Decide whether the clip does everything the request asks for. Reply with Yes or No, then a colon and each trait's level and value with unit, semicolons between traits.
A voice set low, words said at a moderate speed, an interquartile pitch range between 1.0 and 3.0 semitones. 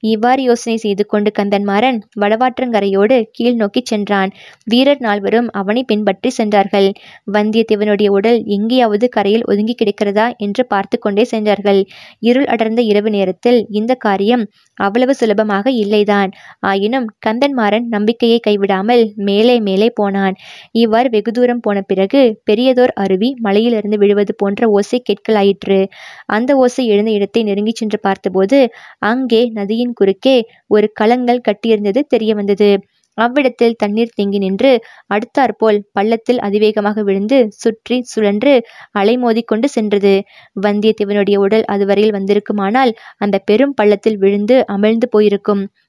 No: high, 215 Hz; average, 120 wpm; average, 2.7 semitones